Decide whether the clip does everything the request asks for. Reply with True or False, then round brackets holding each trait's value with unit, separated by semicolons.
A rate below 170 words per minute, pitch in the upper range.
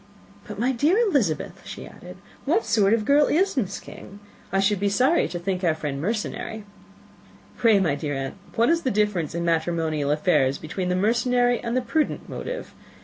False (185 wpm; 205 Hz)